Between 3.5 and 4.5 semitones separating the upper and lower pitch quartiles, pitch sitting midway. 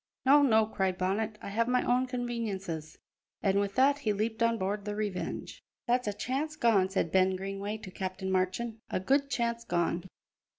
No: average, 3.9 semitones; high, 210 Hz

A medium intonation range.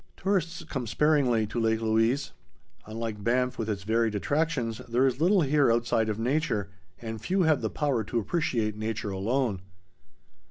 Yes: average, 4.6 semitones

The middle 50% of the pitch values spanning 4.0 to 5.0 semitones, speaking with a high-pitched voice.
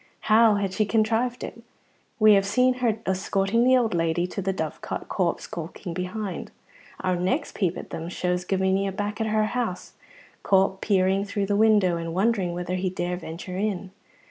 No: average, 3.0 semitones; high, 195 Hz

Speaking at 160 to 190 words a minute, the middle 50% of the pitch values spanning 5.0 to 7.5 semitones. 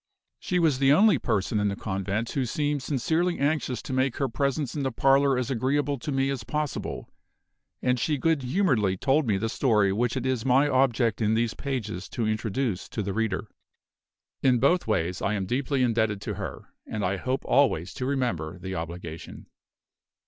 No: average, 185 wpm; average, 4.5 semitones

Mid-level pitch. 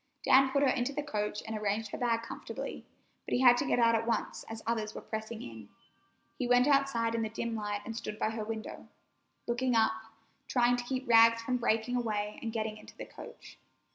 No: high, 230 Hz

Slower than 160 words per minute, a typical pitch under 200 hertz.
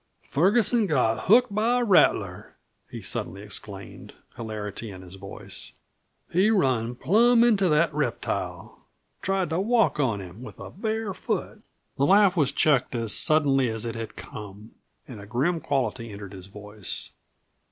Yes: average, 150 wpm; low, 135 Hz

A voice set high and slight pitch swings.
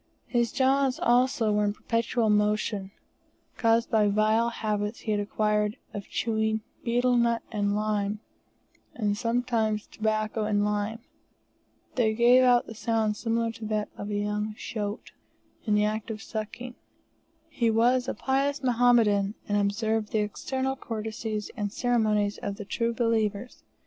Yes: high, 220 Hz; narrow, 2.1 semitones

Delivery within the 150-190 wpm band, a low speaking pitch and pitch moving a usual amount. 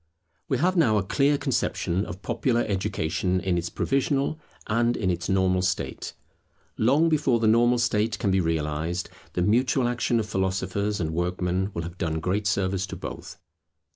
Yes: average, 170 wpm; low, 100 Hz; average, 4.7 semitones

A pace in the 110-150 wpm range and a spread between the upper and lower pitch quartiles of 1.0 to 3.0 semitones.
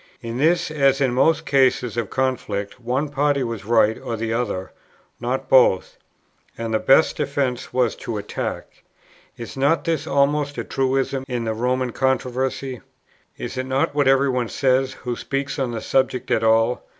No: average, 170 wpm; average, 2.7 semitones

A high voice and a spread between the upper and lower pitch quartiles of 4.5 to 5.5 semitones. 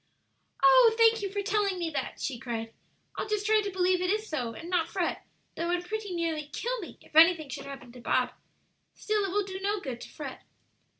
Yes: very high, 360 Hz; average, 5.1 semitones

